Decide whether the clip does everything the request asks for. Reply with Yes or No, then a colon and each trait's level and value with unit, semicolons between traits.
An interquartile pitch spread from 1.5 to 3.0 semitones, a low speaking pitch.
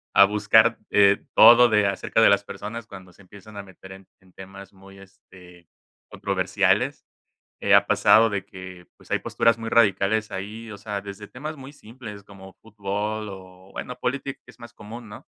Yes: narrow, 2.6 semitones; low, 100 Hz